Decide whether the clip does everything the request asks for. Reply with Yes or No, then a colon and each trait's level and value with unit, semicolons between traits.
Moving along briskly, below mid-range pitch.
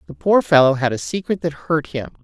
No: fast, 240 wpm; medium, 155 Hz